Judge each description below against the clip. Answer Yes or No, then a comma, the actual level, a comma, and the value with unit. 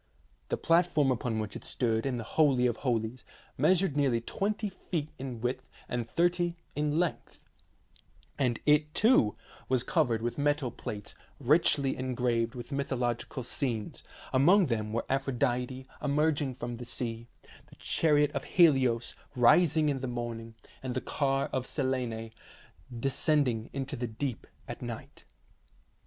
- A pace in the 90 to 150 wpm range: Yes, average, 140 wpm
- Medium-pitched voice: No, low, 130 Hz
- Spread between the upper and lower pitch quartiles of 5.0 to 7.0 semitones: No, average, 3.7 semitones